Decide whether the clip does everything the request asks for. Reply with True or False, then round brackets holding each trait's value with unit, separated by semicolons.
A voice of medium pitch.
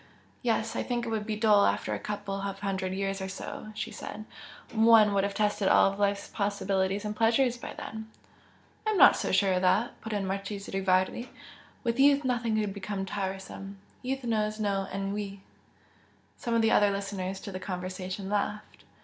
False (205 Hz)